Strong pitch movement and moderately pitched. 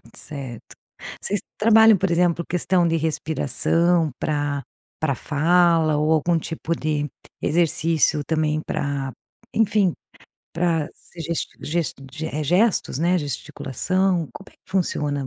No: average, 2.9 semitones; medium, 160 Hz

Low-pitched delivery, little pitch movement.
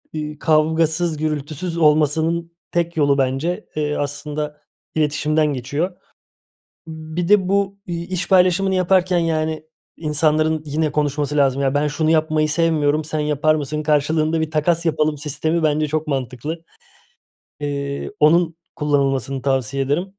No: medium, 155 Hz; narrow, 2.1 semitones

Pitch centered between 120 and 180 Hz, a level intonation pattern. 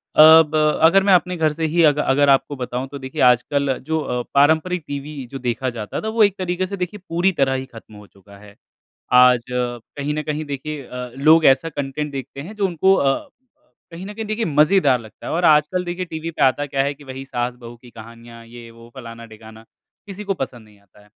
No: medium, 140 Hz; average, 5.0 semitones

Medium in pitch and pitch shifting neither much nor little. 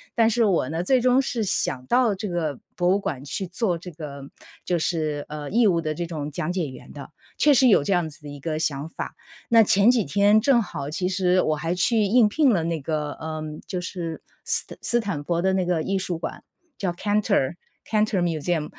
Yes: medium, 175 Hz; average, 5.0 semitones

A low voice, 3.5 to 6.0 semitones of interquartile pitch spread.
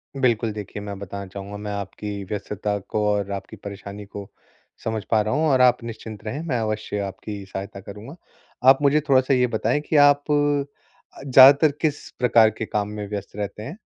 Yes: low, 110 Hz; average, 4.5 semitones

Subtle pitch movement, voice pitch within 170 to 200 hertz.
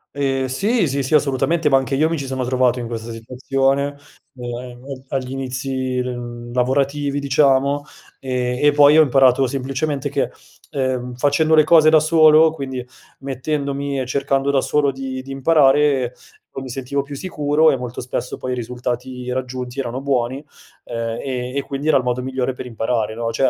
No: narrow, 2.0 semitones; low, 135 Hz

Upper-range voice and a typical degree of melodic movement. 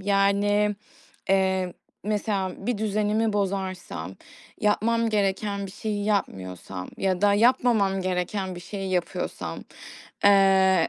No: high, 200 Hz; narrow, 1.8 semitones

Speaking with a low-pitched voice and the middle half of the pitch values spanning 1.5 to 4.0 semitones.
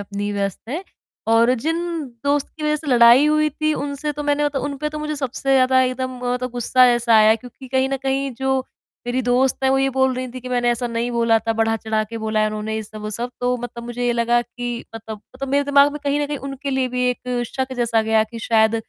No: very high, 250 Hz; average, 2.9 semitones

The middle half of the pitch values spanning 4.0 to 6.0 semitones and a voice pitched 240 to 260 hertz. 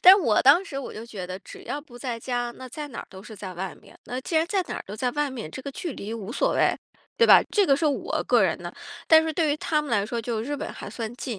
Yes: average, 5.1 semitones; very high, 255 Hz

